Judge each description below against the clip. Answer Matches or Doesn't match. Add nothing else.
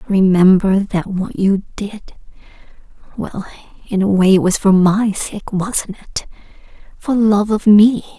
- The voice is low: Doesn't match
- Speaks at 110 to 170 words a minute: Matches